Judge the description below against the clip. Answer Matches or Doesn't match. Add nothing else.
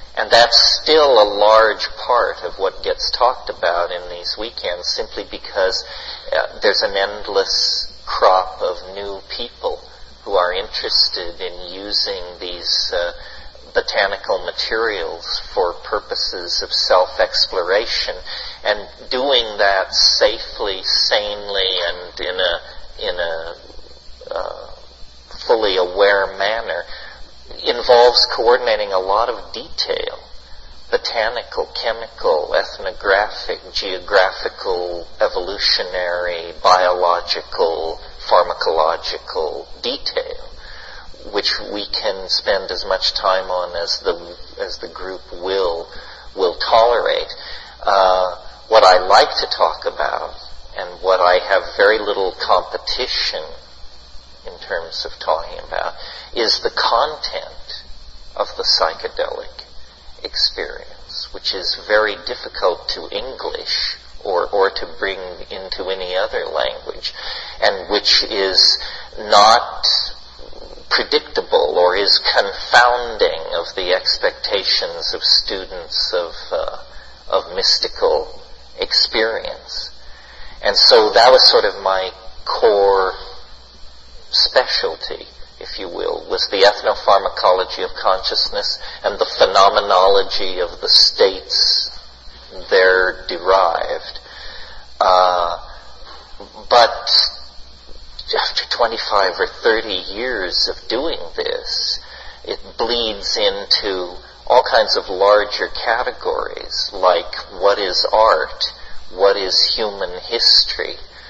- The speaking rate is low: Matches